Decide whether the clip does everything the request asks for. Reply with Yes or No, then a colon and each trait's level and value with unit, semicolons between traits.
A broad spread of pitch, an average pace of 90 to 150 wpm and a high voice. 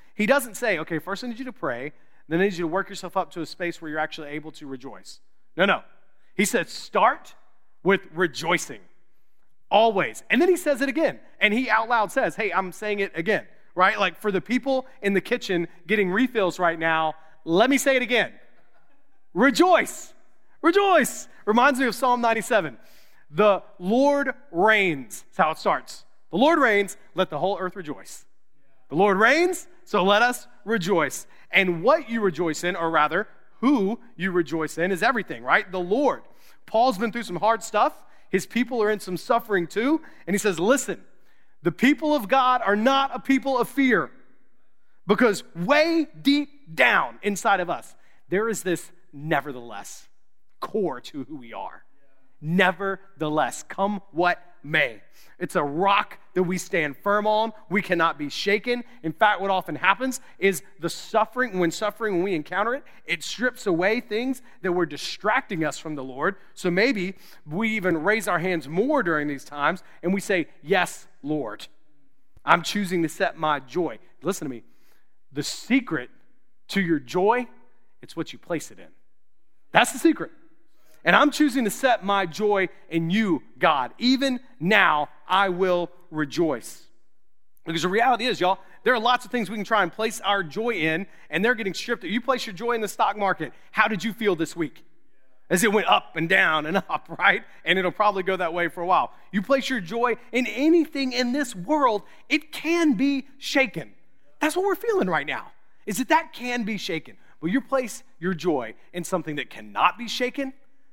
No: wide, 6.2 semitones; average, 185 wpm; high, 200 Hz